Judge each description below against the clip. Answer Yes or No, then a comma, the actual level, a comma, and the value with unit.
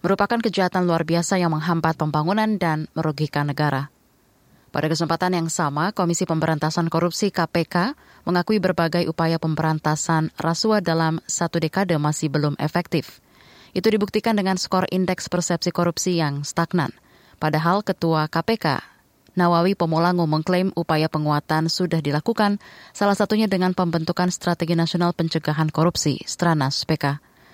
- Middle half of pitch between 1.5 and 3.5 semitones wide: Yes, narrow, 2.5 semitones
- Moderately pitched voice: Yes, medium, 170 Hz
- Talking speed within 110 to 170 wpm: Yes, average, 125 wpm